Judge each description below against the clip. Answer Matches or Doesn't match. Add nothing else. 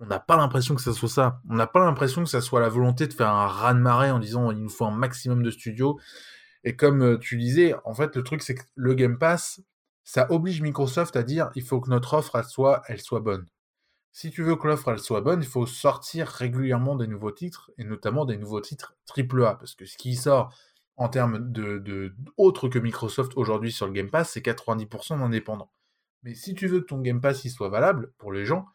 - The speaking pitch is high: Doesn't match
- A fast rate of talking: Matches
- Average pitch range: Matches